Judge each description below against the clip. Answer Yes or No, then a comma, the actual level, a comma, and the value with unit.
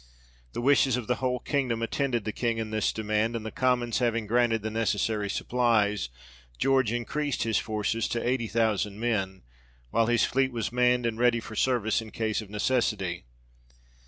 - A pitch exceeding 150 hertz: No, low, 115 Hz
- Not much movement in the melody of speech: Yes, narrow, 2.3 semitones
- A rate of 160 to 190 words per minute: Yes, average, 175 wpm